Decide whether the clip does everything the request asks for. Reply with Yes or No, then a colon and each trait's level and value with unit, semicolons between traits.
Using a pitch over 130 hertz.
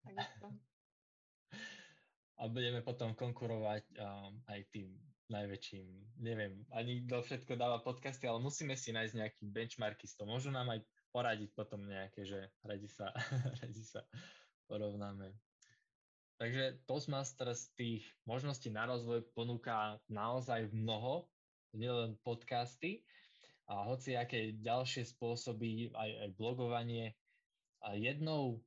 No: low, 115 Hz